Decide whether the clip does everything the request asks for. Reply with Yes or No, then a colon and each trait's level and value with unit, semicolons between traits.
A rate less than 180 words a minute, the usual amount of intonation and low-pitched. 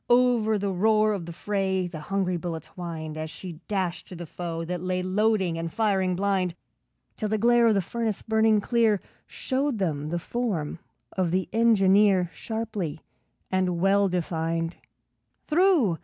No: average, 155 wpm; average, 4.1 semitones; high, 190 Hz